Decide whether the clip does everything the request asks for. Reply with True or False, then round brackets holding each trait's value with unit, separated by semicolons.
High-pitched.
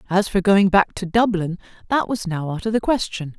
True (195 Hz)